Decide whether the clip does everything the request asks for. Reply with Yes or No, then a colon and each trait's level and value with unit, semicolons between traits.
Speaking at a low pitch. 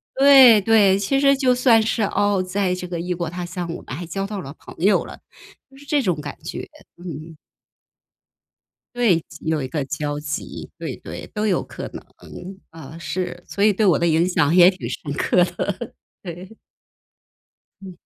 No: medium, 185 Hz